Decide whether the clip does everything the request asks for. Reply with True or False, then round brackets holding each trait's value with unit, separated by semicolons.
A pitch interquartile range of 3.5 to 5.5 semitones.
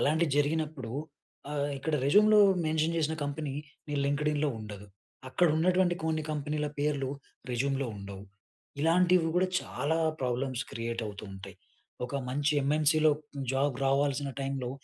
False (2.9 semitones)